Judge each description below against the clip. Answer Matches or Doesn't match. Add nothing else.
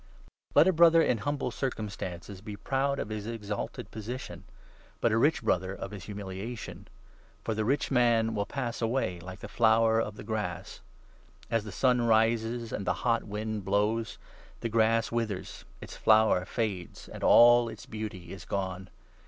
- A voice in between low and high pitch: Doesn't match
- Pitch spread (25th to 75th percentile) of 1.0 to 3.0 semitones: Matches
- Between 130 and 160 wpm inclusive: Doesn't match